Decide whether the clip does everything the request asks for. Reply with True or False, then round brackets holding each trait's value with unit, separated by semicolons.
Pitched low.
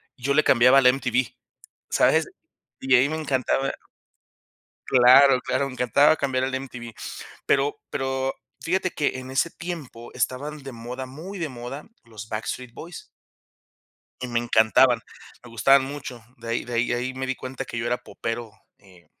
True (130 Hz)